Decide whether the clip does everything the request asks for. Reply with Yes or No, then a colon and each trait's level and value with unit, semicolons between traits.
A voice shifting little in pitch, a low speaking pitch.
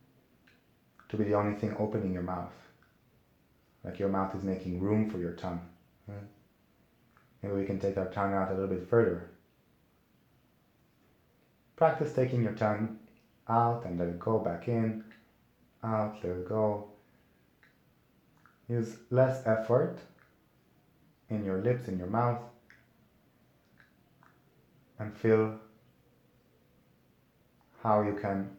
No: average, 3.2 semitones; low, 105 Hz